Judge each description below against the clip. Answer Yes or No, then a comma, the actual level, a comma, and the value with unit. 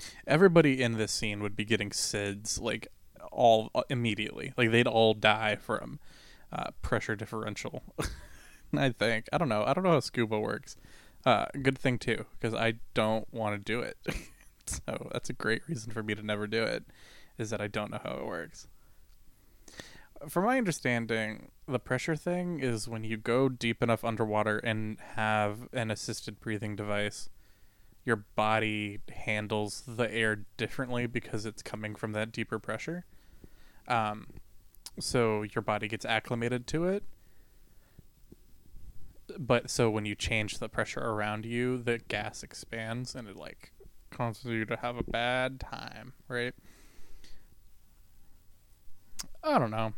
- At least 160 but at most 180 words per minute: No, average, 150 wpm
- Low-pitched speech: Yes, low, 110 Hz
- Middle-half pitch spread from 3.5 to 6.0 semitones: No, narrow, 2.5 semitones